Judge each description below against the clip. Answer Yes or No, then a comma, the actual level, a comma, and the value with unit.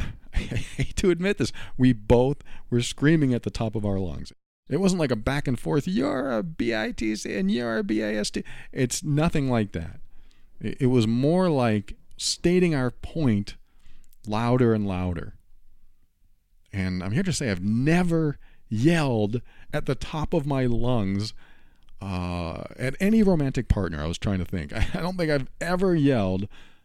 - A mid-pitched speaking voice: No, low, 120 Hz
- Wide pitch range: Yes, wide, 7.4 semitones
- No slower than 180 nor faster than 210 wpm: No, average, 165 wpm